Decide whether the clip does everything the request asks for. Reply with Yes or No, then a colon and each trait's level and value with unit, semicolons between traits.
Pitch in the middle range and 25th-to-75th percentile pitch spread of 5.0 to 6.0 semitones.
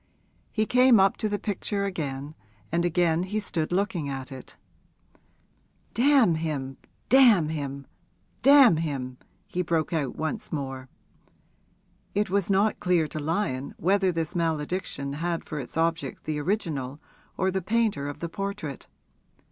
Yes: medium, 165 Hz; average, 5.3 semitones